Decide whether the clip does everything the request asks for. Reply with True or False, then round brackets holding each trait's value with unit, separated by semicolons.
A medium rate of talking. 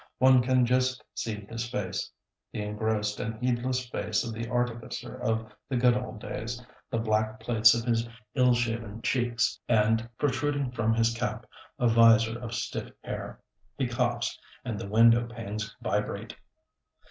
True (155 wpm)